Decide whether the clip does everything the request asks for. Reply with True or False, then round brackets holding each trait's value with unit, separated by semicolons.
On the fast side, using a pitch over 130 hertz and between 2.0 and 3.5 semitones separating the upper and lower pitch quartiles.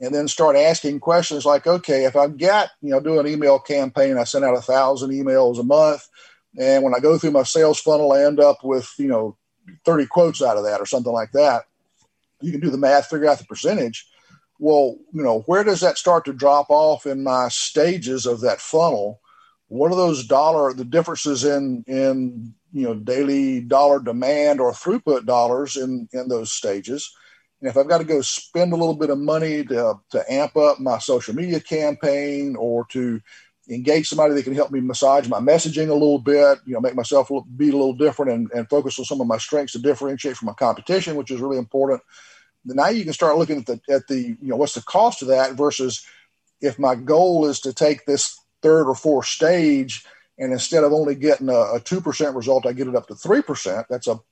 True (220 wpm; 140 Hz; 2.9 semitones)